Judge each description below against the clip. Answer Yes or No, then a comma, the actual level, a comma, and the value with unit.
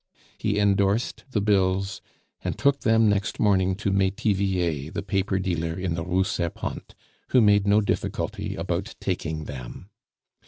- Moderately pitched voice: No, very low, 95 Hz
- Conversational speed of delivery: Yes, average, 145 wpm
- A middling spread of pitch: No, narrow, 2.1 semitones